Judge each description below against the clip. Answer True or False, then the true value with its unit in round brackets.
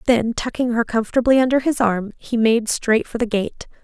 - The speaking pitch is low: False (230 Hz)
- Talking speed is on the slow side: False (205 wpm)